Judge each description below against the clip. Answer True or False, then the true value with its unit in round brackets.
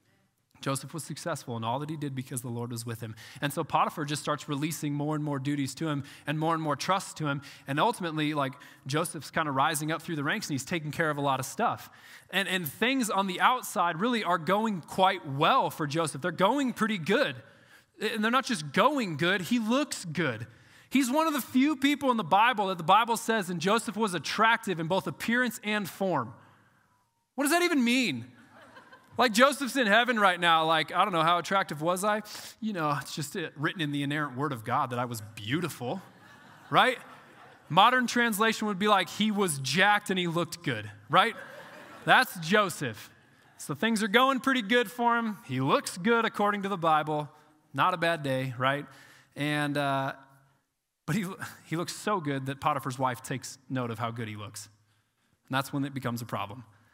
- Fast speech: True (210 wpm)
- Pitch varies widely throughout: True (7.3 semitones)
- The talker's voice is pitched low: False (165 Hz)